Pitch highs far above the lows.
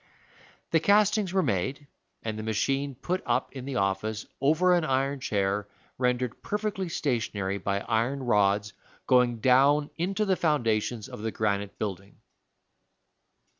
Yes: wide, 6.1 semitones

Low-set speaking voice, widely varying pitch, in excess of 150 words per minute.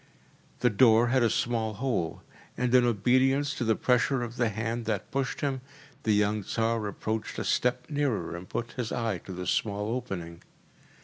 No: low, 115 Hz; average, 3.1 semitones; average, 180 wpm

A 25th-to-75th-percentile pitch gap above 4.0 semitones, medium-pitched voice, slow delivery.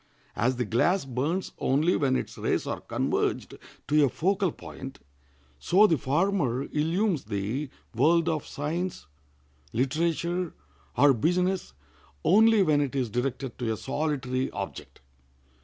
Yes: average, 5.2 semitones; medium, 150 Hz; slow, 130 wpm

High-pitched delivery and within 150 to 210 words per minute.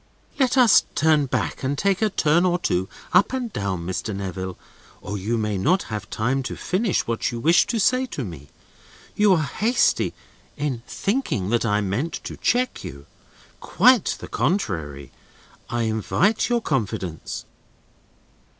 No: low, 135 Hz; average, 155 wpm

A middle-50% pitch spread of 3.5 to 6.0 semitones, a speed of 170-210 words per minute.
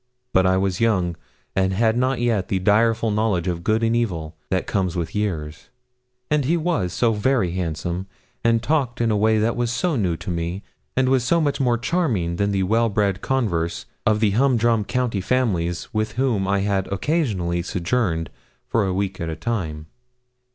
Yes: average, 4.5 semitones; average, 185 wpm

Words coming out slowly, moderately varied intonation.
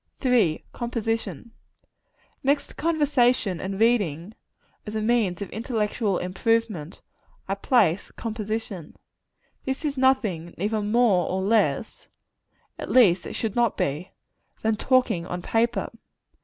Yes: slow, 120 wpm; average, 4.3 semitones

